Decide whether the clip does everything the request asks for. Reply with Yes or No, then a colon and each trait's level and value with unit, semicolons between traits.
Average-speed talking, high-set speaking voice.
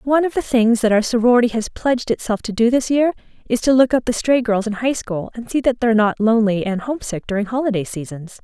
No: fast, 255 wpm; high, 230 Hz